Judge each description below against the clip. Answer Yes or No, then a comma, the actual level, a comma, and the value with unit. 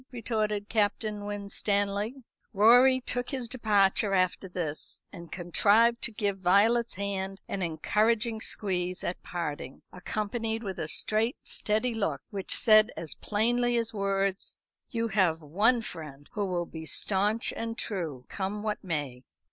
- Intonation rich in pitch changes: No, average, 3.5 semitones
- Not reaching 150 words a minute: Yes, average, 140 wpm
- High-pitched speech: Yes, high, 205 Hz